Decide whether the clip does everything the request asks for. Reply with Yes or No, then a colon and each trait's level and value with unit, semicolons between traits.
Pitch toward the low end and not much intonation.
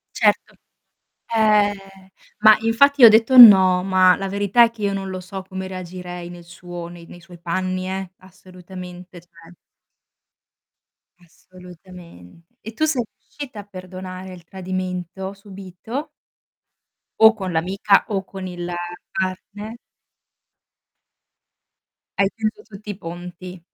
No: medium, 185 Hz; narrow, 2.3 semitones